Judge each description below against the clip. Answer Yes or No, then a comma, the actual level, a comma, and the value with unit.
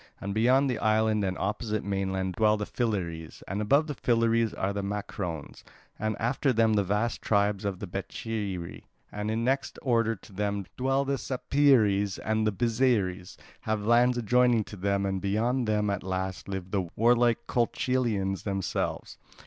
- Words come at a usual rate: Yes, average, 165 wpm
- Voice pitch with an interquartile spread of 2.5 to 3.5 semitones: Yes, average, 3.2 semitones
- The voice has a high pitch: No, low, 105 Hz